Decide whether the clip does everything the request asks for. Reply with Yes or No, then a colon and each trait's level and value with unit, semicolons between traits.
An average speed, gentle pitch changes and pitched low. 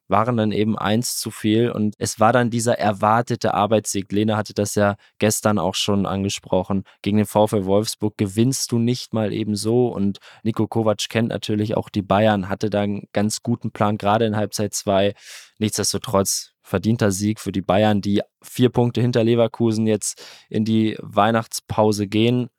Yes: average, 175 wpm; narrow, 1.7 semitones; low, 105 Hz